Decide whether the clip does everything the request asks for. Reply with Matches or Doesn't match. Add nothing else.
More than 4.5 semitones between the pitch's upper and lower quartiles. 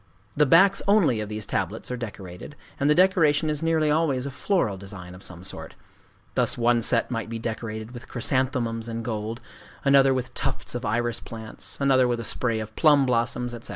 Doesn't match